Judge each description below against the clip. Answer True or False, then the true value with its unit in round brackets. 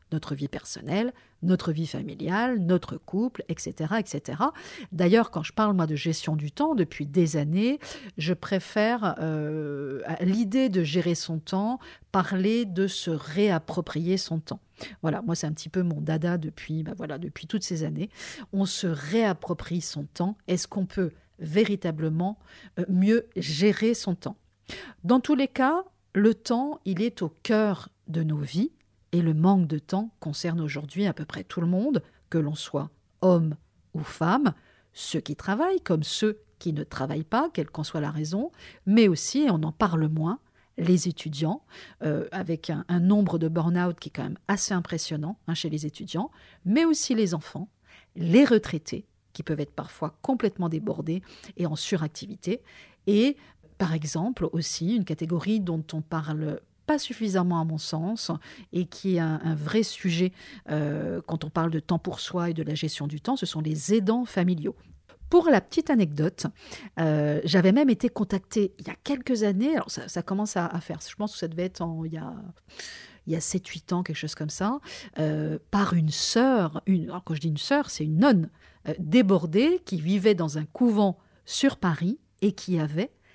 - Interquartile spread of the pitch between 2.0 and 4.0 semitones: False (4.8 semitones)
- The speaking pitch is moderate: True (180 Hz)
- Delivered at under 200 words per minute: True (185 wpm)